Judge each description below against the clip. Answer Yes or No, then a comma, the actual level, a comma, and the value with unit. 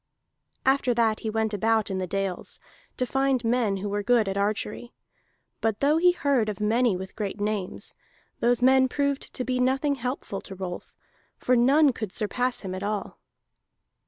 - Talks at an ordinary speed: Yes, average, 175 wpm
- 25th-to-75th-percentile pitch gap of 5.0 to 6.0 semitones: No, average, 3.9 semitones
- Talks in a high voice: Yes, high, 225 Hz